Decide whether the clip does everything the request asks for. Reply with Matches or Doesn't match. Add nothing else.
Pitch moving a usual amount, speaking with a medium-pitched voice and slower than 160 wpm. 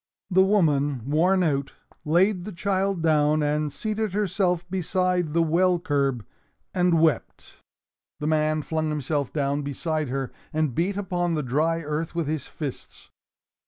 Matches